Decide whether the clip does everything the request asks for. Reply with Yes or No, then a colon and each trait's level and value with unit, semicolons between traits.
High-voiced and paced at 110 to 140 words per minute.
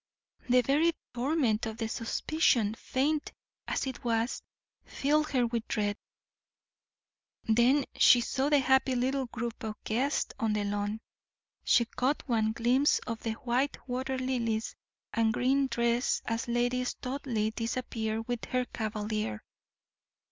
Yes: high, 240 Hz; slow, 135 wpm